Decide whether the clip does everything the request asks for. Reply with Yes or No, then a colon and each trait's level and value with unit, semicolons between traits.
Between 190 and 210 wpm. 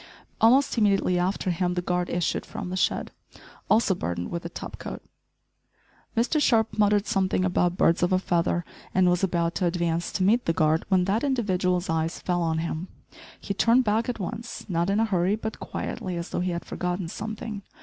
Yes: average, 195 wpm